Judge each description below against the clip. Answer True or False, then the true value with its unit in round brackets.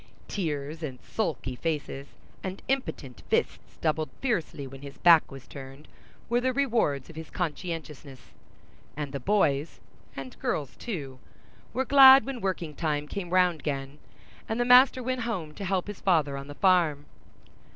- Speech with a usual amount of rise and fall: False (6.4 semitones)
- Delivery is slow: False (150 wpm)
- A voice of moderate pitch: True (160 Hz)